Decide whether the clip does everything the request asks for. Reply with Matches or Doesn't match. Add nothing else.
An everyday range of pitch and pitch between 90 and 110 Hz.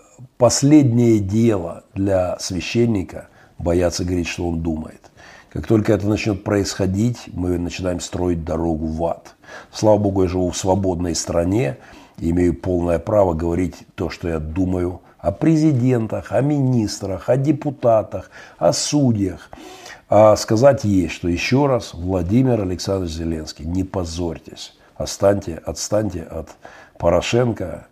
Matches